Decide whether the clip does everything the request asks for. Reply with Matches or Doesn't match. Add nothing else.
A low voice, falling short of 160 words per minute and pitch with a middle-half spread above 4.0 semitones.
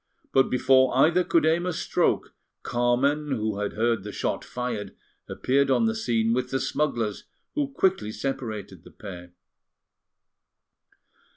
Matches